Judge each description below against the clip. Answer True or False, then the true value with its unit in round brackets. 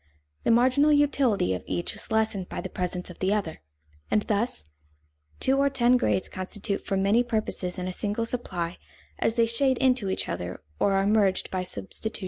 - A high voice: True (210 Hz)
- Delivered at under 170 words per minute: False (180 wpm)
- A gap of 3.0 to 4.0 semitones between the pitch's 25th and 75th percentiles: False (4.5 semitones)